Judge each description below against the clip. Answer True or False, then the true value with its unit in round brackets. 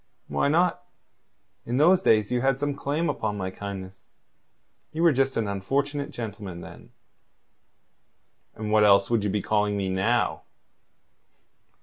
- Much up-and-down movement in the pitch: True (6.0 semitones)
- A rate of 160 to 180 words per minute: False (140 wpm)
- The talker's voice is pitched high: False (110 Hz)